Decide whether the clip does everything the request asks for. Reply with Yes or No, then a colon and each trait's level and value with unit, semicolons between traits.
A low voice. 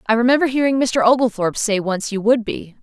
No: high, 230 Hz